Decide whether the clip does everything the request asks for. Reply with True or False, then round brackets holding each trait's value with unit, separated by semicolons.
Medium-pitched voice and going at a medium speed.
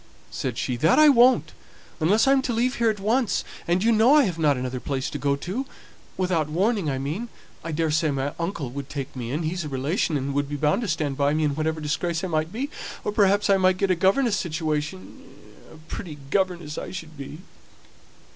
False (165 Hz; 215 wpm)